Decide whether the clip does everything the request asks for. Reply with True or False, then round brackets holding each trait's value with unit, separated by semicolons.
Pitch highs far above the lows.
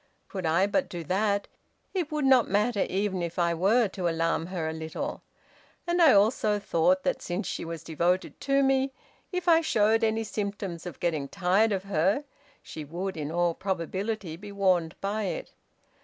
False (4.3 semitones)